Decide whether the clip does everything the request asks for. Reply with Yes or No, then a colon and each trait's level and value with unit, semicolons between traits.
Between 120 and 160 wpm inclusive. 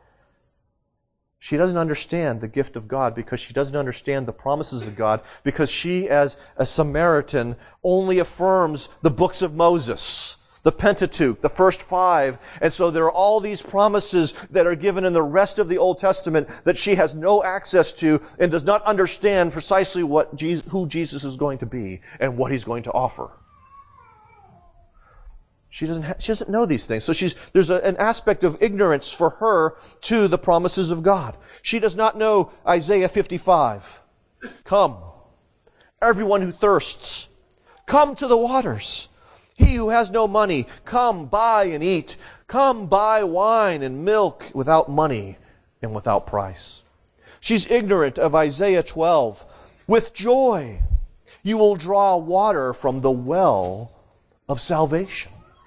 Yes: average, 155 wpm